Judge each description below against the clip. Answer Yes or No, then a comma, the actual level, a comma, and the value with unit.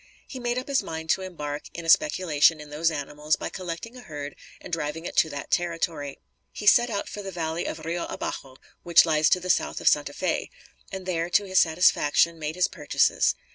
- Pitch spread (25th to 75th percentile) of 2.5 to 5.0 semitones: Yes, average, 3.5 semitones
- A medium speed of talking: No, fast, 215 wpm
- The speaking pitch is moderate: Yes, medium, 165 Hz